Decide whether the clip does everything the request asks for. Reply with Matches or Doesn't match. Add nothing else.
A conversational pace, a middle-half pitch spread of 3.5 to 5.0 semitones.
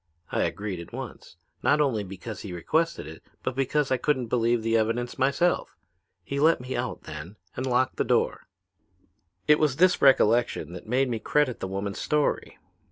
Matches